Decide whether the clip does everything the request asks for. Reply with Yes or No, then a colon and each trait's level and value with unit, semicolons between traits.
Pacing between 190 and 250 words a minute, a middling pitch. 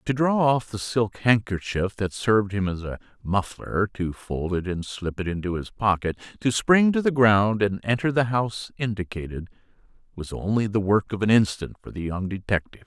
No: average, 195 wpm; low, 105 Hz